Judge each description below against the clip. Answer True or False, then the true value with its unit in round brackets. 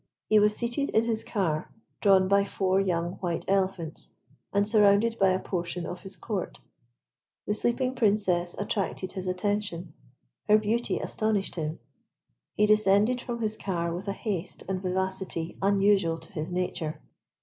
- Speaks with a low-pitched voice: False (195 Hz)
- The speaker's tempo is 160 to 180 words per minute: False (150 wpm)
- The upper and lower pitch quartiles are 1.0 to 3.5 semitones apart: True (2.9 semitones)